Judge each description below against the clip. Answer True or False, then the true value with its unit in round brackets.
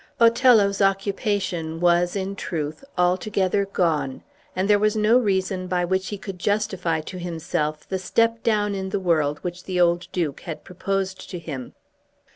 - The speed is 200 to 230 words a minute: False (160 wpm)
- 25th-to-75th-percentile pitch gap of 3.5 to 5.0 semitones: False (2.7 semitones)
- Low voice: False (185 Hz)